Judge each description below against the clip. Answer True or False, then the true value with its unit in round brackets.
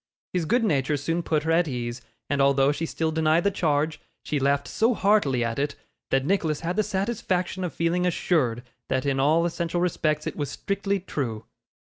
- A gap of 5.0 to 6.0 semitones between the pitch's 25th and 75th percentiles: False (4.3 semitones)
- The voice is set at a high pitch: False (160 Hz)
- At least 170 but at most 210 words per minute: True (195 wpm)